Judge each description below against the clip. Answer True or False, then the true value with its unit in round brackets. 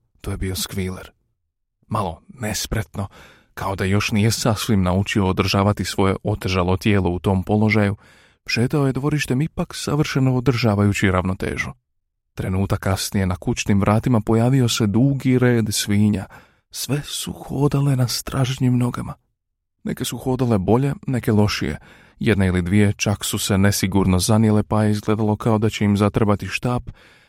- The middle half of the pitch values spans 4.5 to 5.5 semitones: False (3.7 semitones)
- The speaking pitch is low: True (105 Hz)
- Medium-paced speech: True (145 wpm)